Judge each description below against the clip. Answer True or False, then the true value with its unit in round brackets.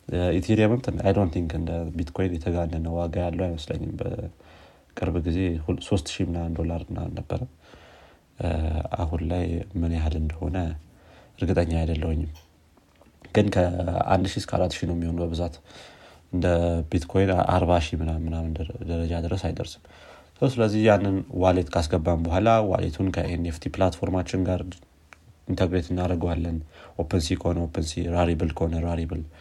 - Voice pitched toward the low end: True (85 Hz)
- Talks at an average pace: False (120 wpm)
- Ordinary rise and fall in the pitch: False (2.0 semitones)